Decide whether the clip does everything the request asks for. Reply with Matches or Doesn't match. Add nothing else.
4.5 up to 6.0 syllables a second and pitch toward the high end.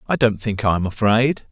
Doesn't match